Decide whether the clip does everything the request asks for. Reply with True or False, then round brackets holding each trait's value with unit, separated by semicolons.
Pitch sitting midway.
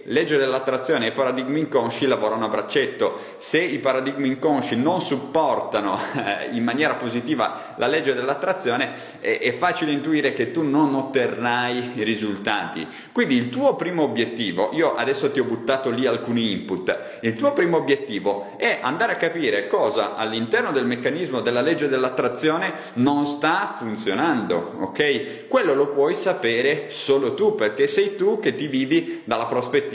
True (155 Hz)